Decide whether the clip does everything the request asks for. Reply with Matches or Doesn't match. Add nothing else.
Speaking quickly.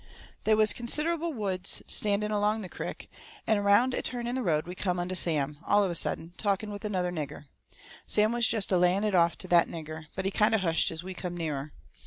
Matches